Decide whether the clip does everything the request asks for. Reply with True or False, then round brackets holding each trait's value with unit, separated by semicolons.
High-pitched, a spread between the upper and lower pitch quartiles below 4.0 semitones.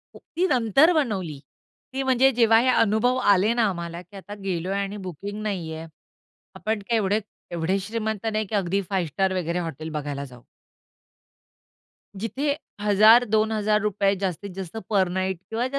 True (200 Hz; 3.5 semitones)